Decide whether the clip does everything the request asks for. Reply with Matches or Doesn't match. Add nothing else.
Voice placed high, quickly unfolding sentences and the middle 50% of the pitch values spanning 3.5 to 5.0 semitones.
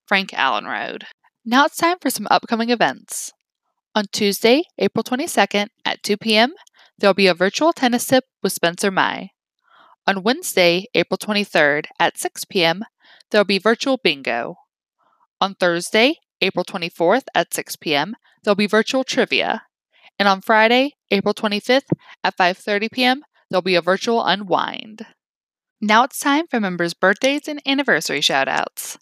Doesn't match